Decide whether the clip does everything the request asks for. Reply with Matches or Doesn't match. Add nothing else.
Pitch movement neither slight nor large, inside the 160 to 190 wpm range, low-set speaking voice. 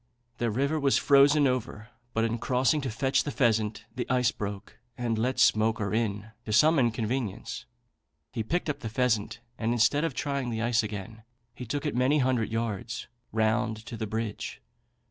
Matches